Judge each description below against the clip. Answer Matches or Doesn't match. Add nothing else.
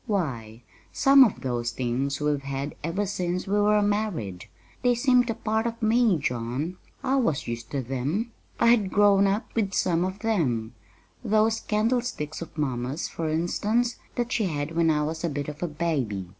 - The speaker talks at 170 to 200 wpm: Matches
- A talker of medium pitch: Matches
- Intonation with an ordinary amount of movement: Doesn't match